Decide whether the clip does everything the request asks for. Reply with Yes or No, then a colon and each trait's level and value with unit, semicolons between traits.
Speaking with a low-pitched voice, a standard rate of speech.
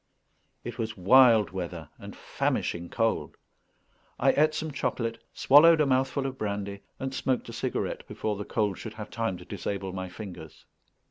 Yes: low, 110 Hz; average, 160 wpm